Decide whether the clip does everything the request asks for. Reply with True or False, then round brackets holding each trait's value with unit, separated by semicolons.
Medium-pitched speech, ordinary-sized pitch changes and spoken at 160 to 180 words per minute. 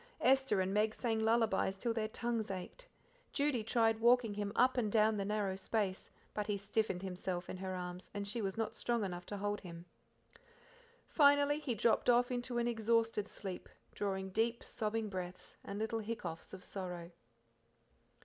False (215 Hz; 3.4 semitones; 170 wpm)